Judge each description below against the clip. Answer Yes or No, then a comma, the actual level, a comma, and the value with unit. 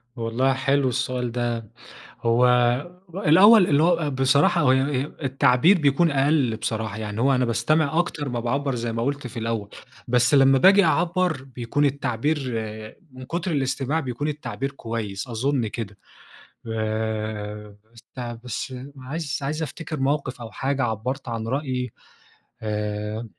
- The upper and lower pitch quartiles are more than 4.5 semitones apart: No, average, 4.1 semitones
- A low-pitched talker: Yes, low, 130 Hz